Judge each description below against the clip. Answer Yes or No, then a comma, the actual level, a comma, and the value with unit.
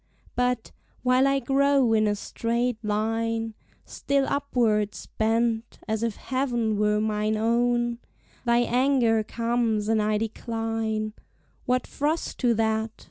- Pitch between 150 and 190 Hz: No, high, 230 Hz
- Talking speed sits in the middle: No, slow, 125 wpm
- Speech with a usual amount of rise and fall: No, narrow, 2.2 semitones